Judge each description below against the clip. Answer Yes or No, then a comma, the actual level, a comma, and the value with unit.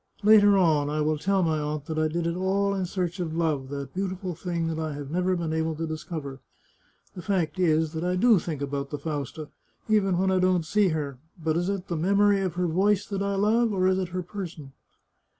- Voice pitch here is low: No, medium, 175 Hz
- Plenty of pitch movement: No, average, 3.4 semitones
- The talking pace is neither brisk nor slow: No, fast, 225 wpm